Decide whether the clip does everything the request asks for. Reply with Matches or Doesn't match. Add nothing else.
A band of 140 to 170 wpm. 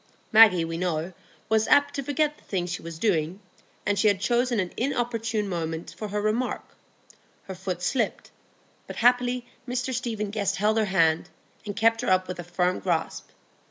Doesn't match